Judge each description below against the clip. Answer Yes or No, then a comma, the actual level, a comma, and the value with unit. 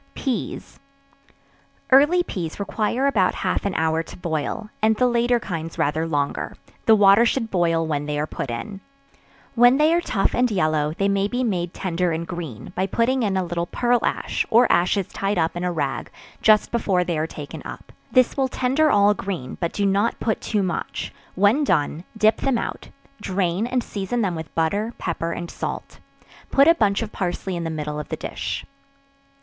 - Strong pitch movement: Yes, wide, 5.7 semitones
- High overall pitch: Yes, high, 195 Hz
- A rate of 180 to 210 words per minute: Yes, average, 190 wpm